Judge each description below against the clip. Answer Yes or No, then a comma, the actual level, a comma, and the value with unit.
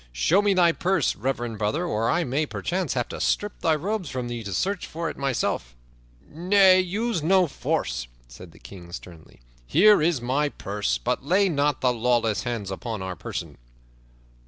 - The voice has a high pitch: No, medium, 140 Hz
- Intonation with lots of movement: Yes, wide, 8.0 semitones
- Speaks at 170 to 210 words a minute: Yes, average, 180 wpm